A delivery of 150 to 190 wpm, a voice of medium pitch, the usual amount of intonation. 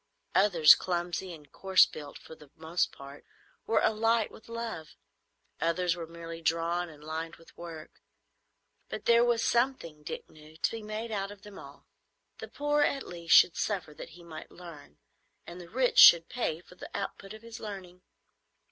Yes: average, 175 wpm; medium, 175 Hz; average, 4.7 semitones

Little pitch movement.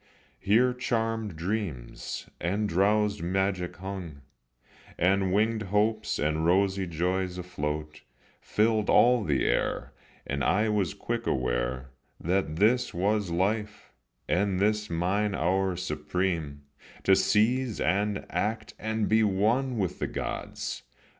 No: average, 3.7 semitones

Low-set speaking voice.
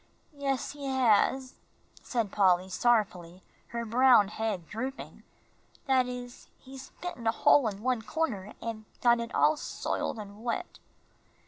No: high, 235 Hz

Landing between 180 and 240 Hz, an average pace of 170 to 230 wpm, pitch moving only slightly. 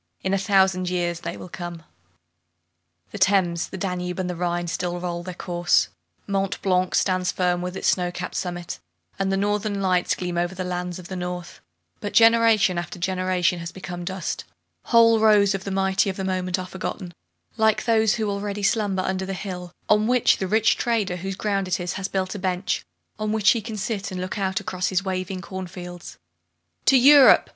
Yes: medium, 185 Hz; average, 200 wpm; narrow, 2.0 semitones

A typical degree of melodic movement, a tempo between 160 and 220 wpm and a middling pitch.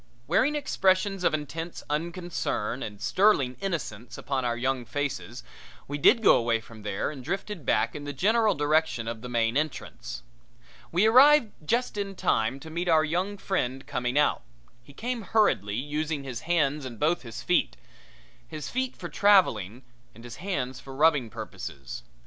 No: wide, 7.4 semitones; average, 165 wpm; medium, 145 Hz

